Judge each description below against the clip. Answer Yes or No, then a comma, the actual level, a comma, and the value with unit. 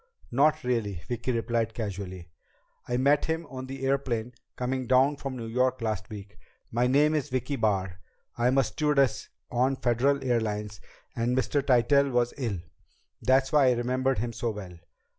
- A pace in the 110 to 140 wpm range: No, average, 160 wpm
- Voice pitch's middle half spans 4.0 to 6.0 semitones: No, average, 3.1 semitones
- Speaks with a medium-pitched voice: No, low, 125 Hz